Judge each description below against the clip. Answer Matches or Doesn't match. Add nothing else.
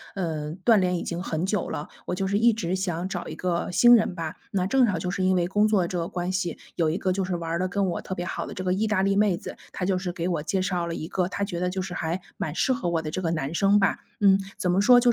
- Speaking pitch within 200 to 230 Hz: Doesn't match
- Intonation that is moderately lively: Doesn't match